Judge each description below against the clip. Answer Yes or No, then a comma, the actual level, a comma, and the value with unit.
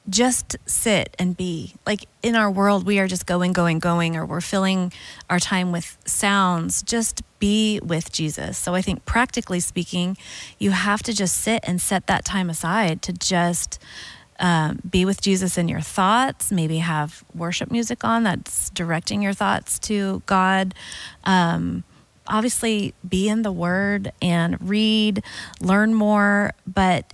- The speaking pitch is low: No, high, 190 Hz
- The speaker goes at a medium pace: Yes, average, 155 wpm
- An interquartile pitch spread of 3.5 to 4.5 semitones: No, average, 2.8 semitones